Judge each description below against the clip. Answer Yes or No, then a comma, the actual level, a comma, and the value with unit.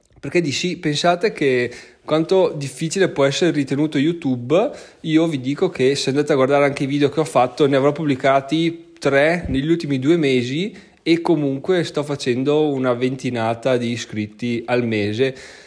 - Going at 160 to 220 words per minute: Yes, average, 165 wpm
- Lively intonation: No, average, 3.7 semitones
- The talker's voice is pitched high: No, medium, 140 Hz